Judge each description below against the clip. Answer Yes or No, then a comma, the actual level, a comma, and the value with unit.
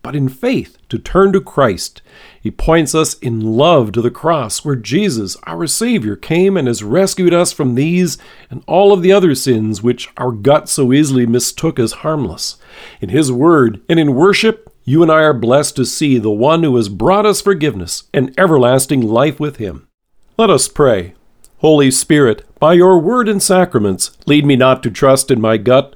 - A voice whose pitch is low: No, medium, 145 Hz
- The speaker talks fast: No, average, 190 wpm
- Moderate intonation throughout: No, wide, 5.7 semitones